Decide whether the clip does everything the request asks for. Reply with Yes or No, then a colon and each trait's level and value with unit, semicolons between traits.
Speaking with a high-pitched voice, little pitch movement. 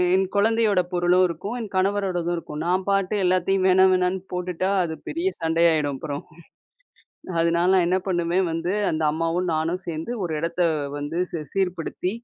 No: medium, 180 Hz; narrow, 2.2 semitones